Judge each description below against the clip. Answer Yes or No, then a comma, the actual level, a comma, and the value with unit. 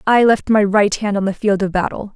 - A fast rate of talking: Yes, fast, 280 wpm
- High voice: Yes, high, 205 Hz